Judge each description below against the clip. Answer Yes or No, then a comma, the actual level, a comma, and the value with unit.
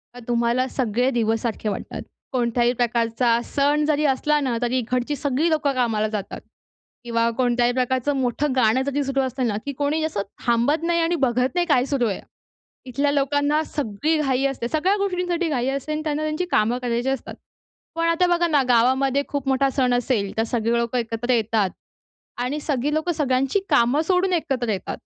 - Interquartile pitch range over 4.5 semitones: No, average, 3.8 semitones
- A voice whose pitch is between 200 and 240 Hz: No, very high, 260 Hz